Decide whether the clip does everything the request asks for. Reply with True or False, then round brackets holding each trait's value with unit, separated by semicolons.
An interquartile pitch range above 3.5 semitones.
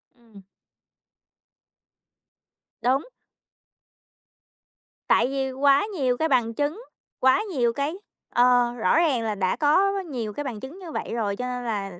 True (4.0 semitones)